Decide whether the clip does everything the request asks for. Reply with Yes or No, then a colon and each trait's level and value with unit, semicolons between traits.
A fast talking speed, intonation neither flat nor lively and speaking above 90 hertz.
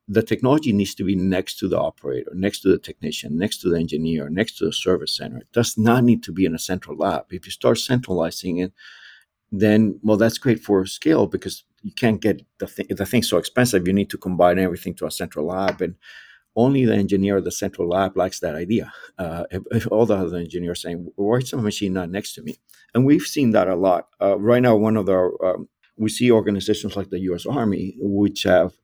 Yes: fast, 235 wpm; average, 3.4 semitones; low, 100 Hz